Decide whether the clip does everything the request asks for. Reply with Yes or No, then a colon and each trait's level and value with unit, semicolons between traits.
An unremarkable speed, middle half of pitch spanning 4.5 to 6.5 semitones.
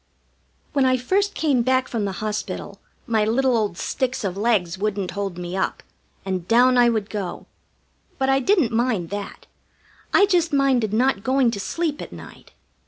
Yes: average, 170 wpm; average, 4.8 semitones